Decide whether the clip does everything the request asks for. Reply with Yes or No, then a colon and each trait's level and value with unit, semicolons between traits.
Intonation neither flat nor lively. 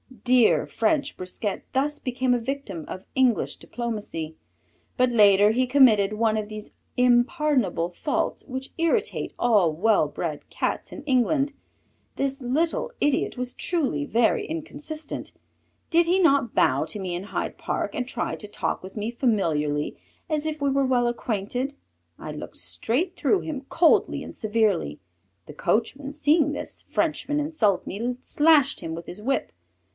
No: wide, 5.7 semitones